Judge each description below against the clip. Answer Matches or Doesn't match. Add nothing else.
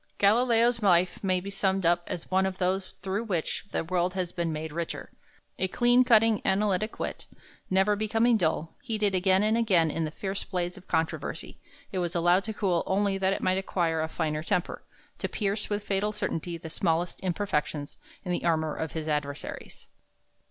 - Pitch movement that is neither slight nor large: Matches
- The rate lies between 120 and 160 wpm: Doesn't match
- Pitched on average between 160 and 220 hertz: Matches